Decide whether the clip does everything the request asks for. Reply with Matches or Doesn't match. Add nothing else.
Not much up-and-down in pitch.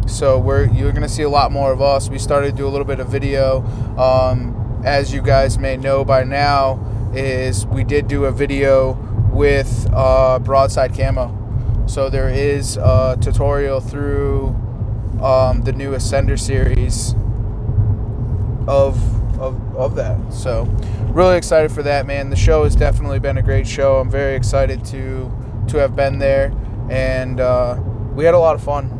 Doesn't match